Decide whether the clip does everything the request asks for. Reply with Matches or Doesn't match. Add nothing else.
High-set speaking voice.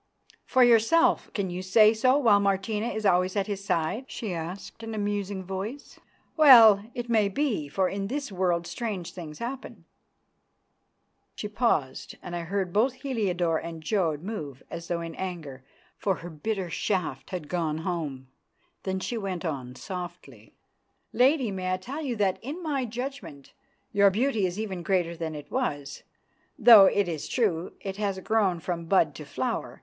Matches